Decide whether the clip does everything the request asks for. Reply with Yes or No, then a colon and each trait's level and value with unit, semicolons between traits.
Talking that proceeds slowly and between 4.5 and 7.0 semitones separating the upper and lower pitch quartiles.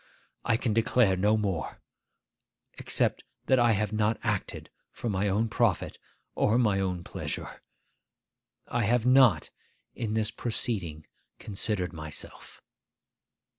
No: slow, 120 wpm; average, 3.2 semitones